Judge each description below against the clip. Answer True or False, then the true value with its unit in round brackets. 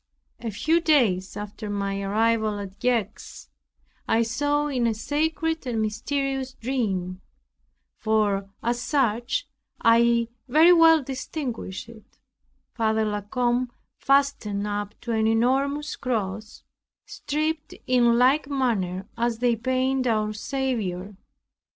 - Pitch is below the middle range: False (235 Hz)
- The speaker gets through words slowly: True (115 wpm)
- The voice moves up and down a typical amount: True (4.2 semitones)